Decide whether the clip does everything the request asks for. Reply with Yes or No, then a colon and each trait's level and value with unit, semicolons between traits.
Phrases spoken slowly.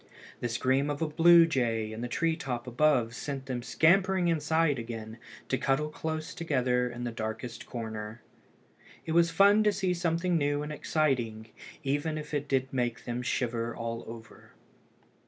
No: average, 165 wpm